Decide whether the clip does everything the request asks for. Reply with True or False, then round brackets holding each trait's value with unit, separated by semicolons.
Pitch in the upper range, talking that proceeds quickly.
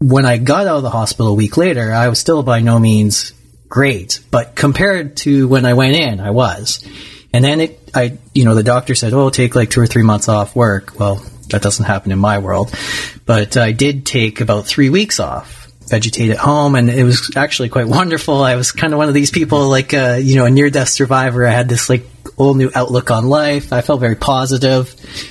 False (125 Hz; 230 wpm)